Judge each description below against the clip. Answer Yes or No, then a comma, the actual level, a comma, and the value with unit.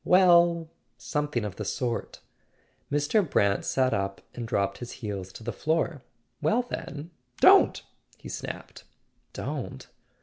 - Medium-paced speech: No, slow, 125 wpm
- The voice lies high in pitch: No, low, 135 Hz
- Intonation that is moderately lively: No, wide, 7.7 semitones